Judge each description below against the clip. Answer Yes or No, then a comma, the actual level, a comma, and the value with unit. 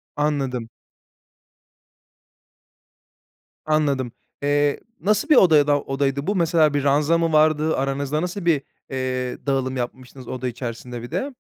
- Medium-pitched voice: Yes, medium, 145 Hz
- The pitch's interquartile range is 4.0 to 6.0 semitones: No, average, 3.1 semitones